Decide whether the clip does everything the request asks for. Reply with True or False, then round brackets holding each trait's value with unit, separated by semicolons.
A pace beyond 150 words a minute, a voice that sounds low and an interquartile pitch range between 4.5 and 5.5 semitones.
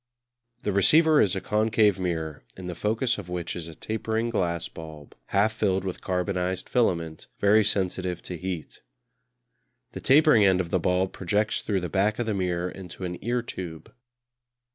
False (170 wpm; 95 Hz; 3.4 semitones)